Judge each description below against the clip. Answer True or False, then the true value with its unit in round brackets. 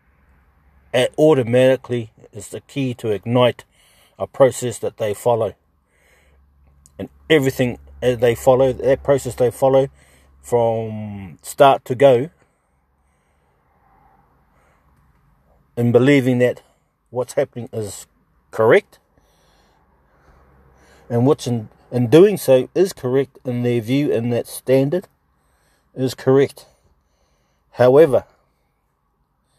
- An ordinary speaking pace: False (95 wpm)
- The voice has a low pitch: True (115 Hz)